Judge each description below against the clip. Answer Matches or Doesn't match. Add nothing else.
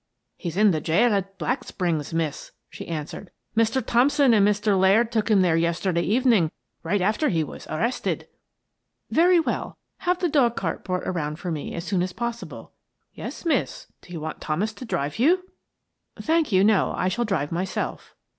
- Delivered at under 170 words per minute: Doesn't match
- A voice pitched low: Doesn't match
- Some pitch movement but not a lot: Doesn't match